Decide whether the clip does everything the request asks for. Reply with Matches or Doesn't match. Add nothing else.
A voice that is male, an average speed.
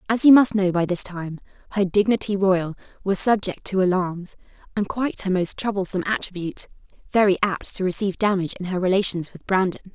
Doesn't match